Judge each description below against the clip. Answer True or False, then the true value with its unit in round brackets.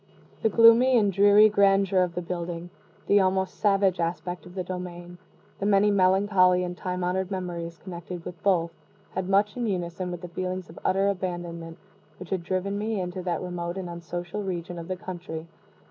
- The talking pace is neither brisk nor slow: True (180 wpm)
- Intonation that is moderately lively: False (2.0 semitones)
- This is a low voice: False (185 Hz)